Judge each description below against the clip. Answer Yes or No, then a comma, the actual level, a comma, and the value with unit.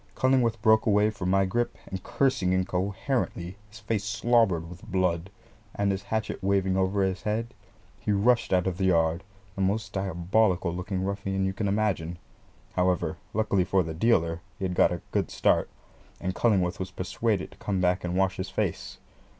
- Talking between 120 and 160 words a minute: No, average, 175 wpm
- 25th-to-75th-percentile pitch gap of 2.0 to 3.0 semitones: Yes, narrow, 2.6 semitones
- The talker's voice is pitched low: Yes, very low, 95 Hz